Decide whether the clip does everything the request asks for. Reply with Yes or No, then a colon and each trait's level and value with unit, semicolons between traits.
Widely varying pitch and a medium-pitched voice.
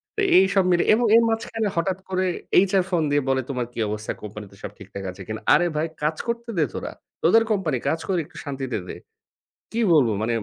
Yes: wide, 8.3 semitones; medium, 160 Hz